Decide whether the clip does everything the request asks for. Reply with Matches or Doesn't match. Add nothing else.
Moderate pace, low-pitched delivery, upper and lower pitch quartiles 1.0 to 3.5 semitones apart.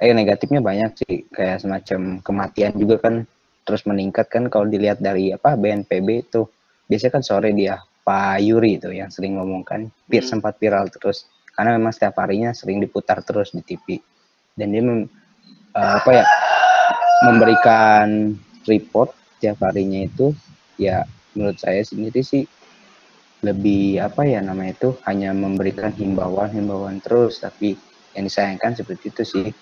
Doesn't match